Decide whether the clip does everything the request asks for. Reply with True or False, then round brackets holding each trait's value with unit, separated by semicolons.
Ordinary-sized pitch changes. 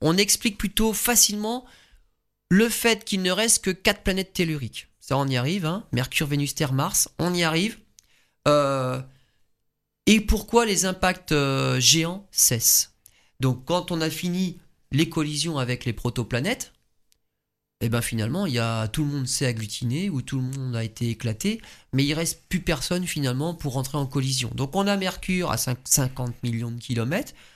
False (6.6 semitones)